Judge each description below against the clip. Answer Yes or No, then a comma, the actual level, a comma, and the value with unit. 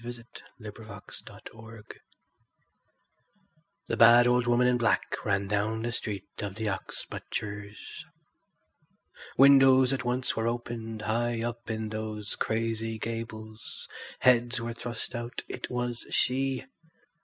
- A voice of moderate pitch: No, low, 115 Hz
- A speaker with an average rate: No, slow, 130 wpm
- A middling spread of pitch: No, narrow, 1.8 semitones